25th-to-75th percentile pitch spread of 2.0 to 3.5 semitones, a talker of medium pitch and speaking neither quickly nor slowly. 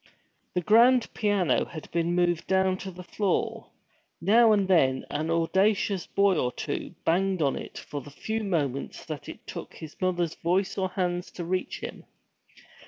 Yes: average, 2.9 semitones; medium, 180 Hz; average, 170 wpm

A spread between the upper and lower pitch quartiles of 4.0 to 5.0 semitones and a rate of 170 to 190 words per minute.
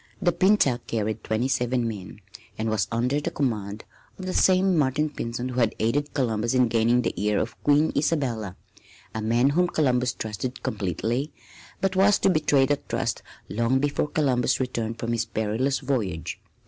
Yes: average, 4.6 semitones; average, 175 wpm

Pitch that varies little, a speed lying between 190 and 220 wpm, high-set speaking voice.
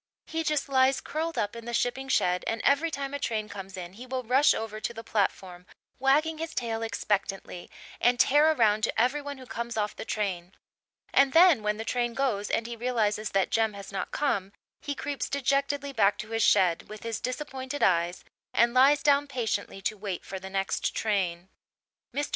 No: average, 5.3 semitones; average, 200 wpm; high, 230 Hz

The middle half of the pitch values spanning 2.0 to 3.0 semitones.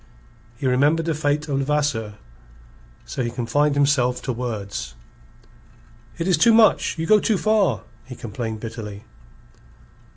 No: average, 5.2 semitones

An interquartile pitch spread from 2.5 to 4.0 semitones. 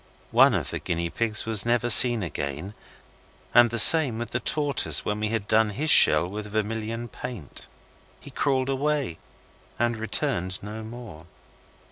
Yes: average, 2.8 semitones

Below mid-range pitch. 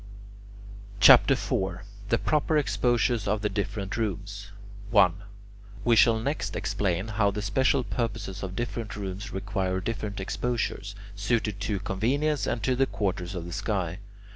Yes: low, 105 Hz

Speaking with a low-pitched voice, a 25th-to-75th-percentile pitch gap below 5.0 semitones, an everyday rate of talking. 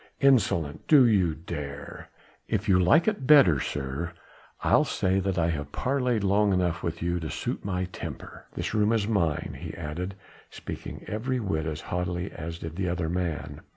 Yes: very low, 90 Hz; average, 4.5 semitones; average, 175 wpm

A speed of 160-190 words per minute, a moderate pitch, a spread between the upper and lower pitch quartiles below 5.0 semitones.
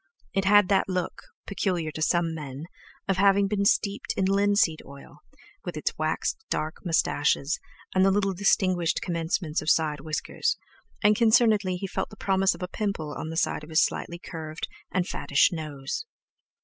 Yes: average, 170 wpm; medium, 180 Hz; average, 3.9 semitones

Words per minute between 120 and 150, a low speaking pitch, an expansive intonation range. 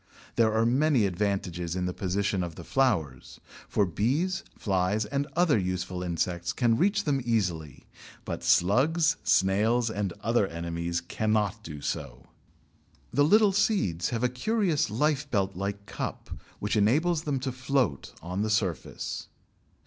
Yes: average, 140 wpm; low, 105 Hz; wide, 7.2 semitones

